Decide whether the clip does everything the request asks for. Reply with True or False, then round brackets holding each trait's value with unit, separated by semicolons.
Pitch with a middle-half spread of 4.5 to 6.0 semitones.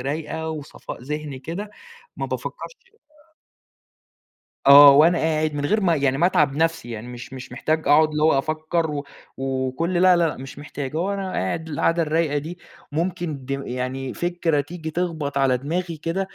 False (3.5 semitones)